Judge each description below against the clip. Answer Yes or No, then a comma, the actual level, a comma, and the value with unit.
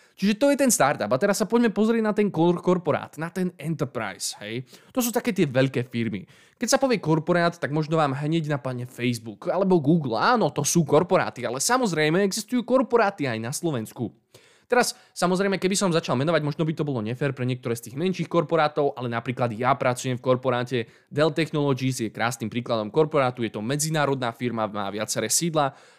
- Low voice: No, medium, 150 Hz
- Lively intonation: Yes, wide, 6.7 semitones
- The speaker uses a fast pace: Yes, fast, 190 wpm